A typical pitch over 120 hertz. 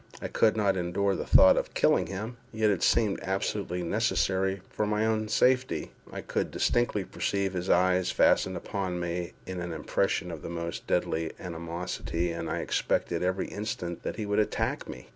No: very low, 95 Hz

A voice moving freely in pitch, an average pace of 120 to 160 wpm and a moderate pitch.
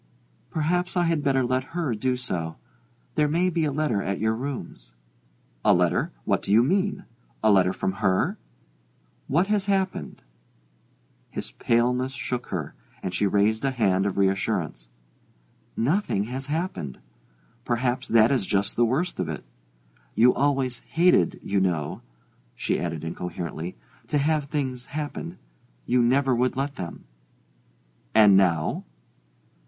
No: wide, 6.8 semitones; average, 140 wpm; low, 125 Hz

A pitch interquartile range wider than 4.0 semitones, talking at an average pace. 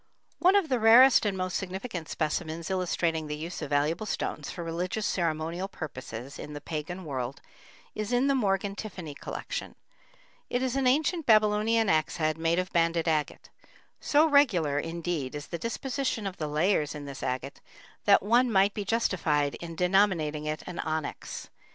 Yes: wide, 5.5 semitones; average, 170 wpm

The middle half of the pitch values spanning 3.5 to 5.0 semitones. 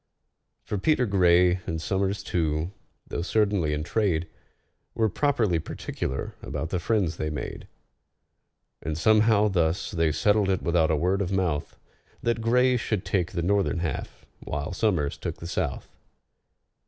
Yes: average, 4.3 semitones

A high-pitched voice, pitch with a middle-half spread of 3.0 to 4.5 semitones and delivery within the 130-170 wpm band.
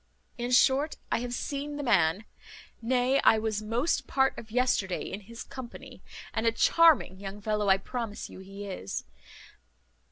Yes: high, 230 Hz; average, 4.1 semitones; average, 160 wpm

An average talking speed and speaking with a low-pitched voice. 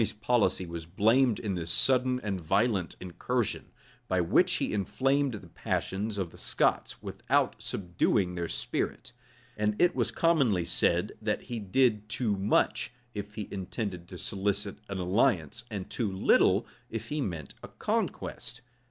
Yes: average, 150 wpm; low, 105 Hz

